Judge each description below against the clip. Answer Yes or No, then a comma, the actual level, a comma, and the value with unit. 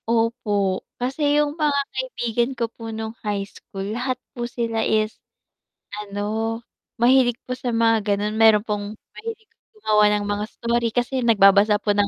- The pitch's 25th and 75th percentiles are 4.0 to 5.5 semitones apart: No, average, 2.7 semitones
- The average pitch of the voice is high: Yes, high, 225 Hz